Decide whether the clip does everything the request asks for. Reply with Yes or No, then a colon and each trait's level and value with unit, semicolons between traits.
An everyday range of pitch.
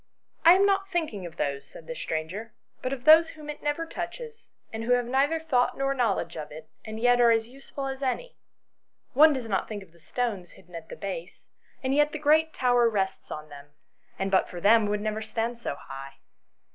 No: wide, 7.4 semitones